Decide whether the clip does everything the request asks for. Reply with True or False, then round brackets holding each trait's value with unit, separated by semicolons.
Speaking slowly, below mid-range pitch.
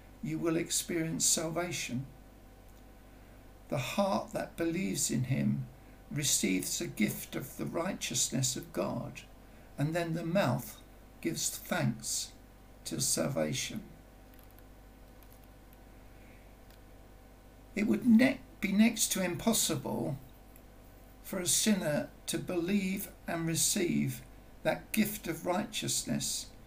False (100 wpm; 165 Hz)